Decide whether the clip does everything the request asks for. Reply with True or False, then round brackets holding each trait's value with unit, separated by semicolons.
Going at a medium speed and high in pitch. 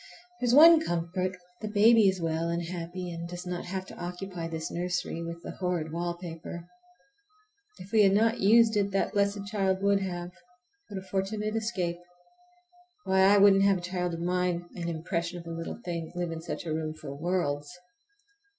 False (180 wpm; 180 Hz)